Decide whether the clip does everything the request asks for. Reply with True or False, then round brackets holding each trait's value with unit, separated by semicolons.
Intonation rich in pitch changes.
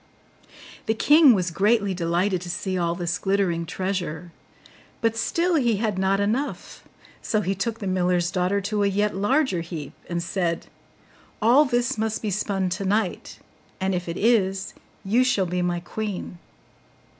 False (3.5 semitones)